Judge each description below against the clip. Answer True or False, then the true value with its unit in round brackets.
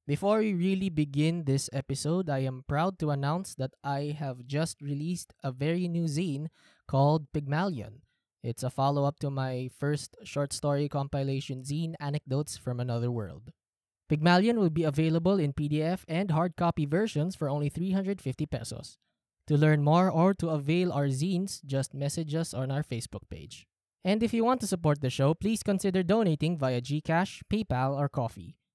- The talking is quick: True (170 wpm)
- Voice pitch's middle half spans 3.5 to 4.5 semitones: True (3.9 semitones)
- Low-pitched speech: False (150 Hz)